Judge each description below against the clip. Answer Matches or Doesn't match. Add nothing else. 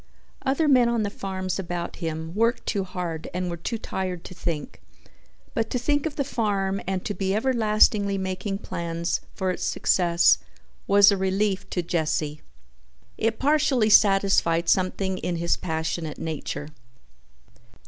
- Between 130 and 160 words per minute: Matches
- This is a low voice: Doesn't match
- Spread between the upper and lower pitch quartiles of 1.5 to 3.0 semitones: Doesn't match